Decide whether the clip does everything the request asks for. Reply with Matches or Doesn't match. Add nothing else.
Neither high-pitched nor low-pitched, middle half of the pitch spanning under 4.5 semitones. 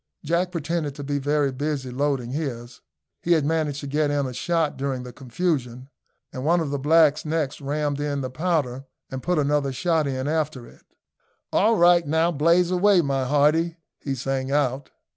Matches